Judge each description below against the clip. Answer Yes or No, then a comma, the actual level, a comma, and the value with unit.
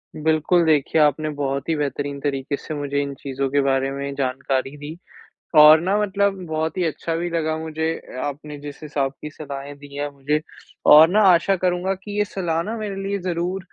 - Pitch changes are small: No, average, 3.4 semitones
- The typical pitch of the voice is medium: Yes, medium, 150 Hz